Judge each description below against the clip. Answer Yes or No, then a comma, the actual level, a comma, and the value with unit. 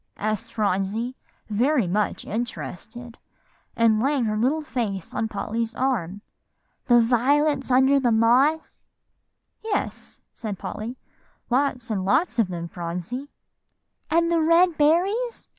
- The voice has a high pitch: Yes, high, 240 Hz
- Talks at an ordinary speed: No, slow, 125 wpm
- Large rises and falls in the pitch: No, average, 5.0 semitones